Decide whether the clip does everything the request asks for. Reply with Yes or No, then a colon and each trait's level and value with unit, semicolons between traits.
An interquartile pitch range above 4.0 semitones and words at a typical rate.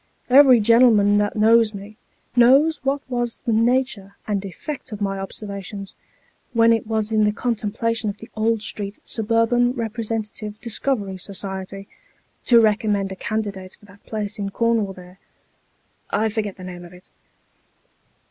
No: narrow, 2.5 semitones; average, 150 wpm